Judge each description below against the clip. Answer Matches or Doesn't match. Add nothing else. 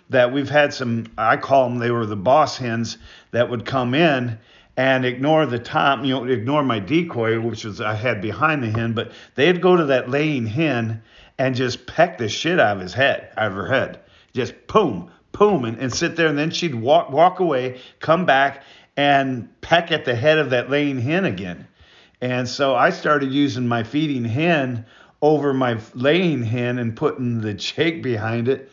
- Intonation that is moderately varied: Matches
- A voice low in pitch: Matches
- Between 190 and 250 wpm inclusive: Matches